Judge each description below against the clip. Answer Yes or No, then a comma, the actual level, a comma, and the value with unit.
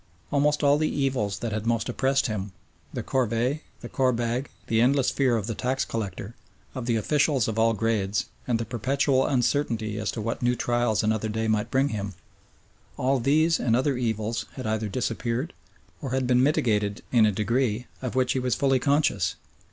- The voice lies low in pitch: Yes, low, 120 Hz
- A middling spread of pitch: Yes, average, 3.3 semitones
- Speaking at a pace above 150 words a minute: Yes, average, 185 wpm